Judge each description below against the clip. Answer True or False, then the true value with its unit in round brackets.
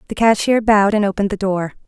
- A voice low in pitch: False (205 Hz)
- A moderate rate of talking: False (225 wpm)